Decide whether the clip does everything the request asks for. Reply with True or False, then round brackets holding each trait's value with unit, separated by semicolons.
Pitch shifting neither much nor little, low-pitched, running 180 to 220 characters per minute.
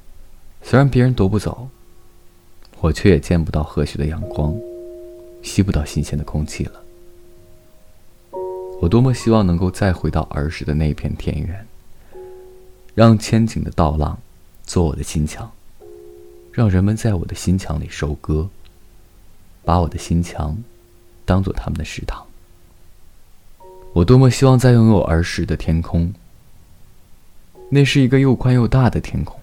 True (3.3 semitones; 90 Hz; 210 characters per minute)